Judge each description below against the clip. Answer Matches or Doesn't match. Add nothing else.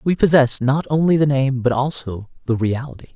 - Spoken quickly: Doesn't match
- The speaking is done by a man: Matches